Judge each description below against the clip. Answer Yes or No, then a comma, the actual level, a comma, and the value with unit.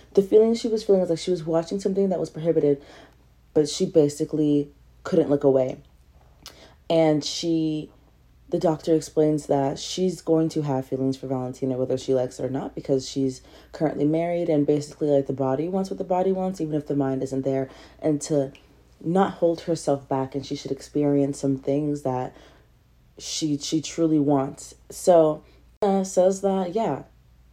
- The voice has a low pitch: No, medium, 150 Hz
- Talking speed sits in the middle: Yes, average, 175 wpm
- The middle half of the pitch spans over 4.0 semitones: No, average, 3.5 semitones